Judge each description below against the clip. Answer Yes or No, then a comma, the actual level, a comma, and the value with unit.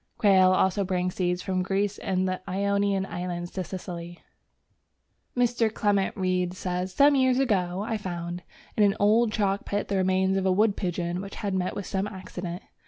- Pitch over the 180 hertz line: Yes, high, 190 Hz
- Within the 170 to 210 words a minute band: Yes, average, 175 wpm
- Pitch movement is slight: Yes, narrow, 2.0 semitones